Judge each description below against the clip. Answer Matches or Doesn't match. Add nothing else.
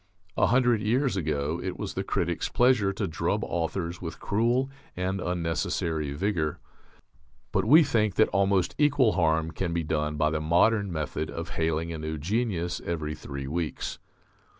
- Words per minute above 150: Matches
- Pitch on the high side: Doesn't match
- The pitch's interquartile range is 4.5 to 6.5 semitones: Matches